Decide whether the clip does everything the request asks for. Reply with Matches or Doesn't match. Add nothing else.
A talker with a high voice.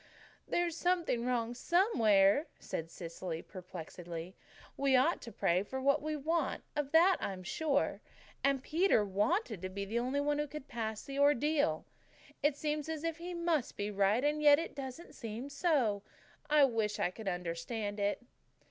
Matches